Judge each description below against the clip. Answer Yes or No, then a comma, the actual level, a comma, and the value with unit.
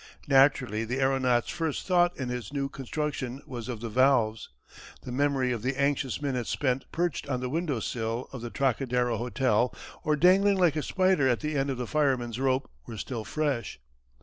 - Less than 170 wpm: No, average, 185 wpm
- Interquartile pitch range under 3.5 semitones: Yes, average, 3.0 semitones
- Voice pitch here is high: No, low, 130 Hz